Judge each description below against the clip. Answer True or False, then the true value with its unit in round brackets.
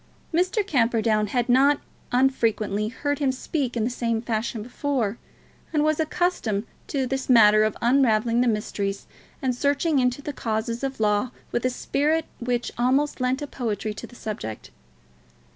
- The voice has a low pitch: False (245 Hz)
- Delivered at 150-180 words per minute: True (155 wpm)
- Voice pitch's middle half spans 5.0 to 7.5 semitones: False (4.0 semitones)